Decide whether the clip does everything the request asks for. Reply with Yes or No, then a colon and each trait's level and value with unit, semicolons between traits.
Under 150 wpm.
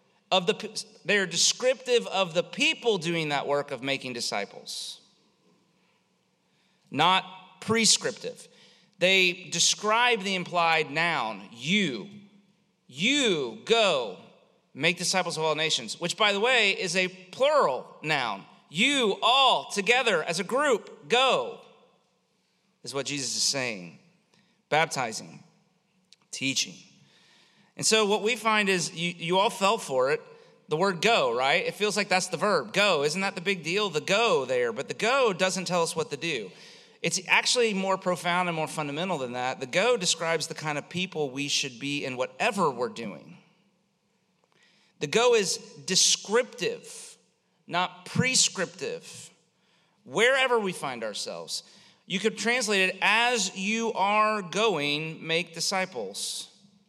Yes: average, 140 wpm